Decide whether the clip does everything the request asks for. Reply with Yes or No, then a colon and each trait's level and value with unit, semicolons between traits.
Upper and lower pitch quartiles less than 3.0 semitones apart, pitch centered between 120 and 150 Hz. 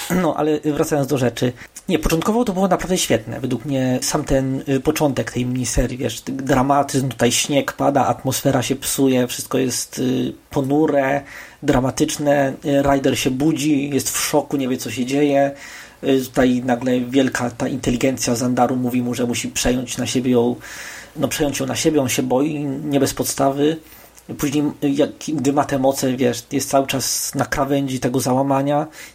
Yes: narrow, 2.4 semitones; low, 135 Hz